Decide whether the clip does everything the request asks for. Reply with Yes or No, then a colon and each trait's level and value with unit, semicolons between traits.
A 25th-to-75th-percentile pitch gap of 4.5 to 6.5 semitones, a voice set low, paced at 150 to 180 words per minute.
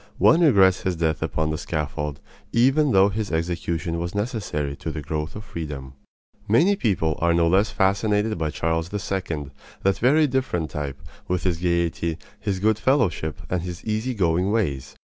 Yes: average, 4.8 semitones; very low, 90 Hz; average, 165 wpm